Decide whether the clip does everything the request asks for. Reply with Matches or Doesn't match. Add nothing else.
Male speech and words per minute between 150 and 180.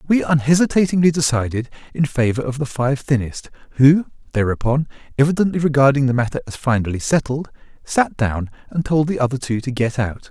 Matches